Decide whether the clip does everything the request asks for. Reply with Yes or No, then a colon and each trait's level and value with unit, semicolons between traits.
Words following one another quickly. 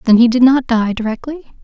Yes: fast, 220 wpm